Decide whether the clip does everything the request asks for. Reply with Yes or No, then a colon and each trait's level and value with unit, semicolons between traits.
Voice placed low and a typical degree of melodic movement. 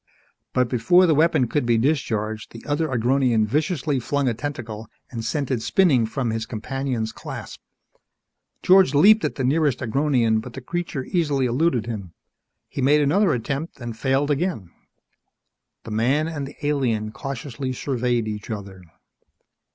Yes: low, 130 Hz; average, 4.5 semitones